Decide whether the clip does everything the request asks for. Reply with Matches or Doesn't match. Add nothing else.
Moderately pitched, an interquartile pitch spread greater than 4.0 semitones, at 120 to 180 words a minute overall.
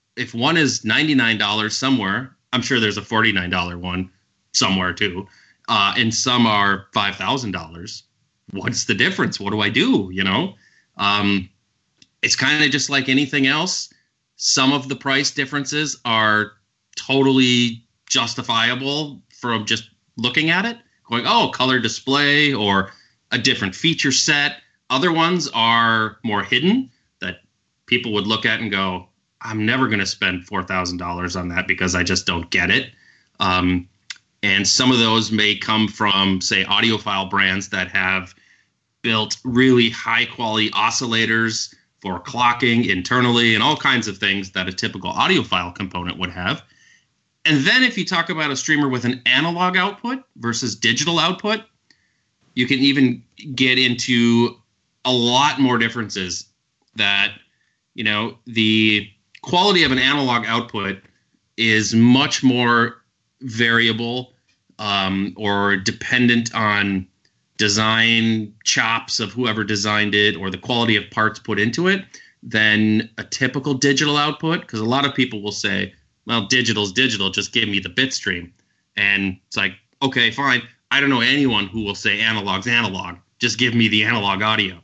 Doesn't match